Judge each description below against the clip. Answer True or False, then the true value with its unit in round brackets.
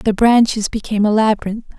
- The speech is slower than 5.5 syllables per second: False (6.1 syllables/s)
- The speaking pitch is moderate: False (215 Hz)